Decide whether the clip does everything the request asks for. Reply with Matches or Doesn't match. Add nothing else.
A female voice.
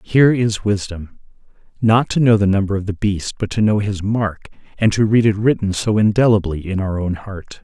Doesn't match